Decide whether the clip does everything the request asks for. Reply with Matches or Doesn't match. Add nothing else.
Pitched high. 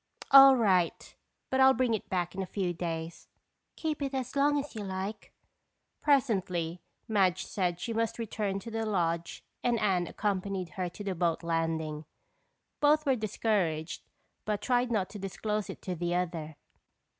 Matches